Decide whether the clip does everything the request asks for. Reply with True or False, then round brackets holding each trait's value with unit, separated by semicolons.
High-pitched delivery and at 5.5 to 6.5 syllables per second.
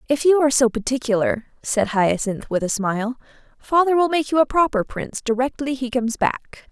True (250 Hz; 5.6 syllables/s)